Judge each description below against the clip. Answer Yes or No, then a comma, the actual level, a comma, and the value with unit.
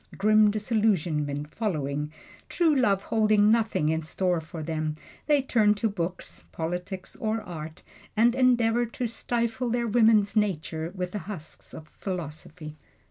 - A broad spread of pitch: Yes, wide, 5.9 semitones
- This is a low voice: No, high, 200 Hz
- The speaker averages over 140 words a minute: No, slow, 135 wpm